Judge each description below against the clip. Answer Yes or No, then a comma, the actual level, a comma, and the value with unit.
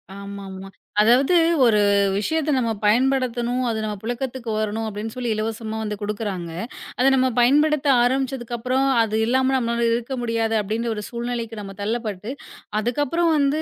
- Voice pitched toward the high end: Yes, high, 235 Hz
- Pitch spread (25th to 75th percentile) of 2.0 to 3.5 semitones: Yes, average, 3.1 semitones